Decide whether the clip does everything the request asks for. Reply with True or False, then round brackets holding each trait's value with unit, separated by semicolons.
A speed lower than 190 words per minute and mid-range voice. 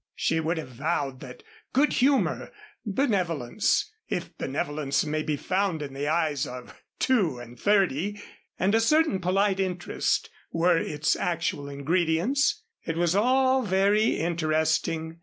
True (135 wpm; 170 Hz)